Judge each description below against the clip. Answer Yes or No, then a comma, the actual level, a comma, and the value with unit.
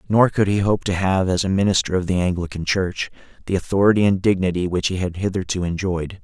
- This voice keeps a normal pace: No, fast, 210 wpm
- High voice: No, very low, 95 Hz